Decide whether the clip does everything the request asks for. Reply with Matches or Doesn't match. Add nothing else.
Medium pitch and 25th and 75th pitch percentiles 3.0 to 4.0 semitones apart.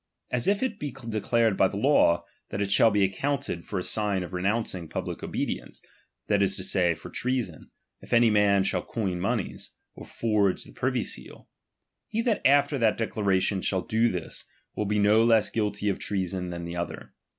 Doesn't match